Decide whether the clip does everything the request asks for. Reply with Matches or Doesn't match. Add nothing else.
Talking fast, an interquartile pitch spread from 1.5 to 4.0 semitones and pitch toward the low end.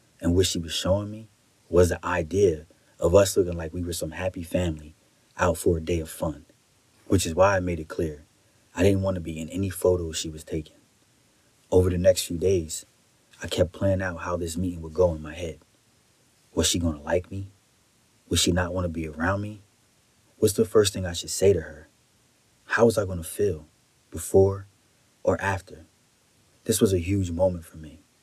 Matches